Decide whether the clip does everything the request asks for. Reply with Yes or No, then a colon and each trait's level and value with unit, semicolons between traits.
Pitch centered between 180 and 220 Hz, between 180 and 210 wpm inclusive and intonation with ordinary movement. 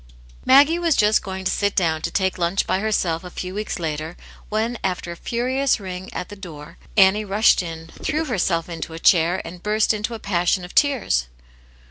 Yes: high, 190 Hz; average, 195 wpm; average, 3.9 semitones